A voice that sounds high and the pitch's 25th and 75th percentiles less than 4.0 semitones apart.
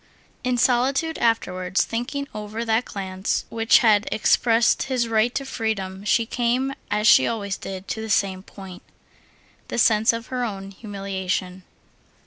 Yes: high, 220 Hz; average, 3.5 semitones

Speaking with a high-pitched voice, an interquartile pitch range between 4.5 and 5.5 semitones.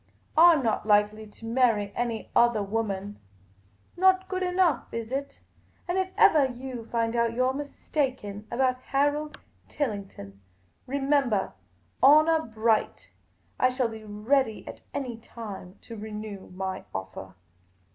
Yes: high, 230 Hz; average, 4.9 semitones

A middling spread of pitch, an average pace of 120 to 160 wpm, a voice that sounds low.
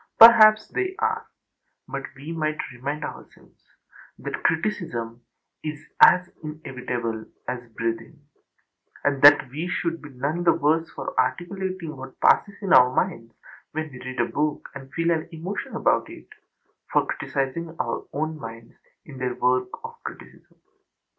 No: average, 4.9 semitones; average, 145 wpm; medium, 150 Hz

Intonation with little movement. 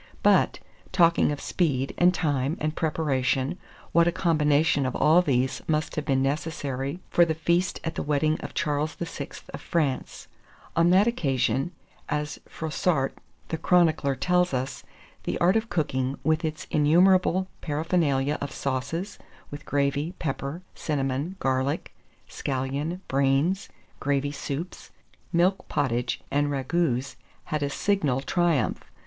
No: average, 3.8 semitones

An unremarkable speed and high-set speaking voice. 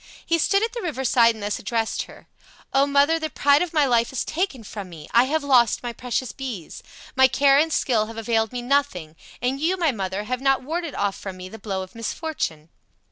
No: fast, 225 wpm; very high, 250 Hz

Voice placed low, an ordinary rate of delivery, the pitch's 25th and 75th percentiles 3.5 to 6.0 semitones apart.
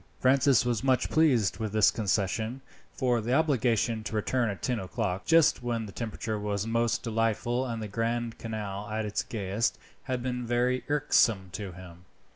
No: low, 115 Hz; average, 170 wpm; average, 2.9 semitones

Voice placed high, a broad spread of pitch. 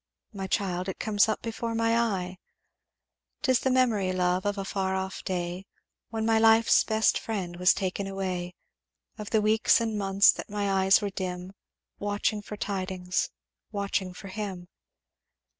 No: high, 195 Hz; average, 2.8 semitones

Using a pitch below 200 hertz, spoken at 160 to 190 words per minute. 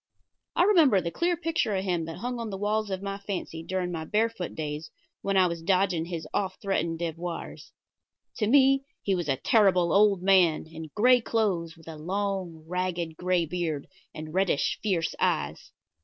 Yes: medium, 185 Hz; average, 180 wpm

